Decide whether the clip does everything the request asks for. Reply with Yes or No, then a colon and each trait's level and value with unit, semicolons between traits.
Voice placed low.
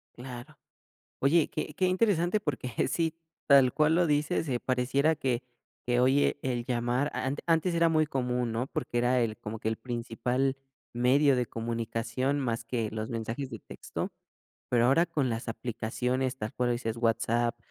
Yes: low, 125 Hz